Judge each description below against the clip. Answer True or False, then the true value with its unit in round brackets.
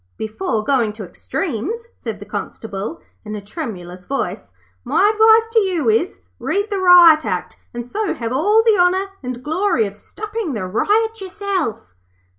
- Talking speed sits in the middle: True (160 wpm)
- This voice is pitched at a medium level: False (330 Hz)